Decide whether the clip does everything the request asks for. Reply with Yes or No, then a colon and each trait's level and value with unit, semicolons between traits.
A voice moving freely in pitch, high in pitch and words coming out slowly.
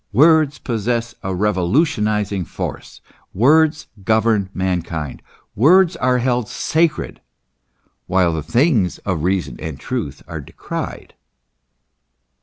No: wide, 6.8 semitones; low, 110 Hz; slow, 105 wpm